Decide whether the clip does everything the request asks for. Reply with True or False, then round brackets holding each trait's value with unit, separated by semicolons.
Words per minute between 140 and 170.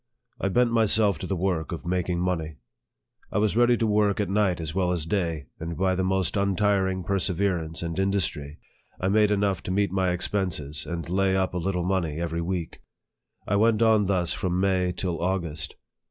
False (190 wpm)